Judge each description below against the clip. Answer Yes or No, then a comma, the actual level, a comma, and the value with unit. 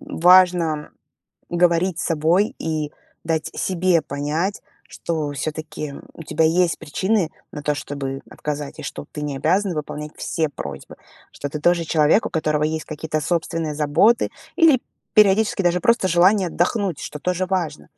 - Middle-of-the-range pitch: Yes, medium, 165 Hz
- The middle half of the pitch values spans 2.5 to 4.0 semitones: Yes, average, 3.4 semitones